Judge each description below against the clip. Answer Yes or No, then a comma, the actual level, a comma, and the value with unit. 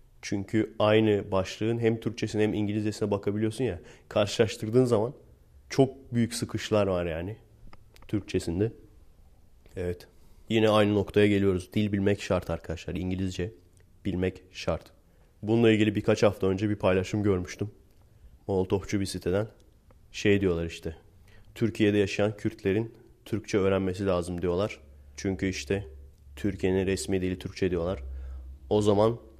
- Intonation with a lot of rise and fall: No, average, 2.9 semitones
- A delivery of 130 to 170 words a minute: No, average, 120 wpm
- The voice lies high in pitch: No, low, 100 Hz